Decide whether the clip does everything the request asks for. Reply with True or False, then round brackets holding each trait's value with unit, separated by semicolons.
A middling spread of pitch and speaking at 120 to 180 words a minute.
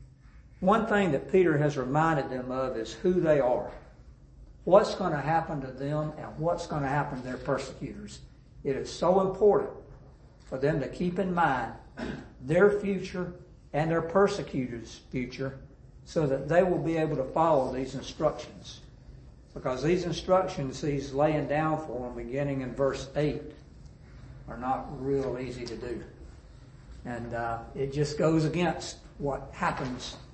True (4.1 semitones; 155 wpm)